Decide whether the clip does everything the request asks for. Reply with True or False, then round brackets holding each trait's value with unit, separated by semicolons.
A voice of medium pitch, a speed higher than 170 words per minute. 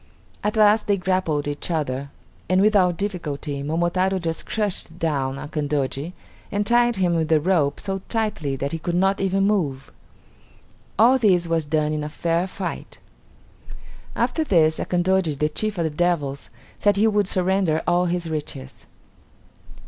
False (175 Hz; 155 wpm)